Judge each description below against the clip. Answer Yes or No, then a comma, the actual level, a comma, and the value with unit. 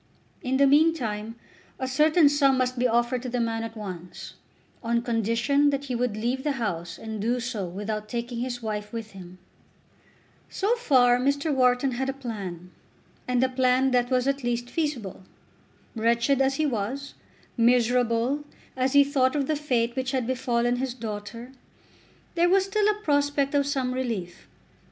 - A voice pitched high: Yes, very high, 250 Hz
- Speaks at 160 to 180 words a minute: Yes, average, 170 wpm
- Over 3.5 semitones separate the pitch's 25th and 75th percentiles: No, average, 3.2 semitones